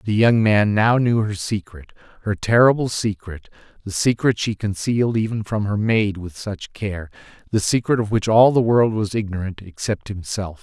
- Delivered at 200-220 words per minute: No, average, 175 wpm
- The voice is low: Yes, low, 105 Hz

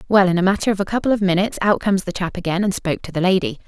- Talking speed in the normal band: No, fast, 310 wpm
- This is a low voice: No, high, 190 Hz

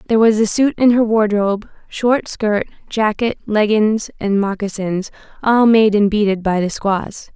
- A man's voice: No, female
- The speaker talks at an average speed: Yes, average, 165 wpm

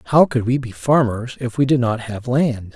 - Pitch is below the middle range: Yes, low, 125 Hz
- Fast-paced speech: Yes, fast, 240 wpm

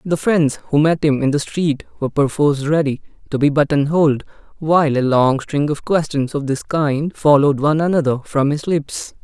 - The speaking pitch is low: No, medium, 145 Hz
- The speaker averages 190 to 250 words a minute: Yes, average, 195 wpm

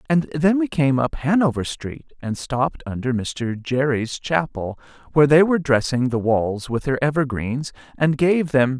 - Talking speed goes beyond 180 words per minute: No, average, 170 wpm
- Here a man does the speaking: Yes, male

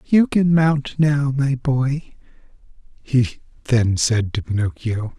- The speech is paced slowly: Yes, slow, 125 wpm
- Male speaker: Yes, male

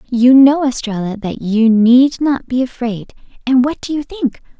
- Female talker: Yes, female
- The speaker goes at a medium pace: Yes, average, 185 wpm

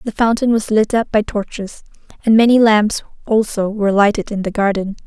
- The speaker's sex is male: No, female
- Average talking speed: Yes, average, 190 wpm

